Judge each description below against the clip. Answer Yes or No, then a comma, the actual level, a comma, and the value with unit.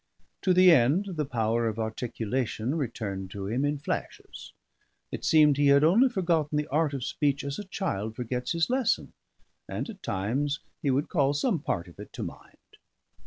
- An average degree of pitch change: No, wide, 5.7 semitones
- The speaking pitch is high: No, medium, 140 Hz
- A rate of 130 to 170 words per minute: No, average, 180 wpm